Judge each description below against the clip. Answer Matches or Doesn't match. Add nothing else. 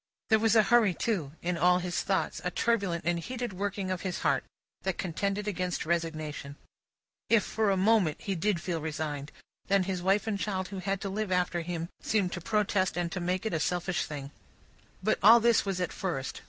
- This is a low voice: Doesn't match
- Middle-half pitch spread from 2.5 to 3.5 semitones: Matches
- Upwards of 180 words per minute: Matches